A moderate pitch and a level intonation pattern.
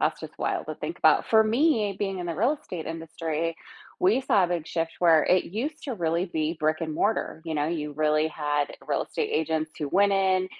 No: medium, 170 Hz; average, 4.0 semitones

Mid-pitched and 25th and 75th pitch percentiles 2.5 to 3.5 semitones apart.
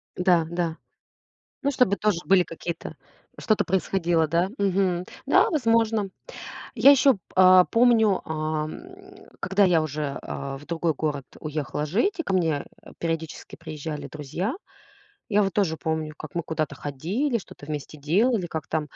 No: medium, 170 Hz; average, 4.4 semitones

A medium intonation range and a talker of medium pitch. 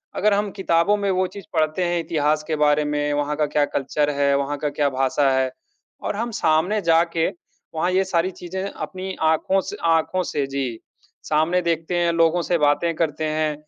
Yes: average, 3.6 semitones; medium, 165 Hz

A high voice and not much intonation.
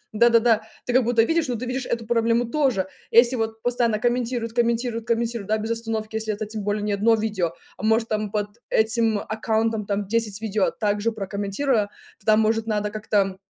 Yes: high, 225 Hz; narrow, 1.8 semitones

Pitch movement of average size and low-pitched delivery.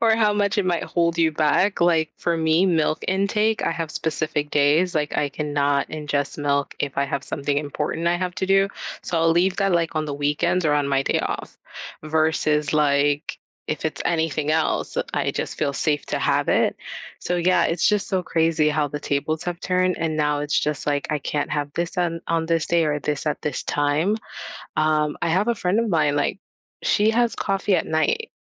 No: average, 3.2 semitones; medium, 160 Hz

